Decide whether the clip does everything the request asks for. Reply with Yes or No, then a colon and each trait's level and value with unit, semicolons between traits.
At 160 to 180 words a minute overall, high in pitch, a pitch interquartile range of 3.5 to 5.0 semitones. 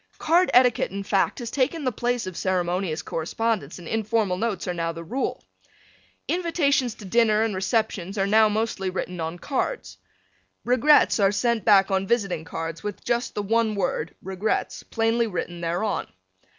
Yes: average, 165 wpm; high, 210 Hz; average, 4.3 semitones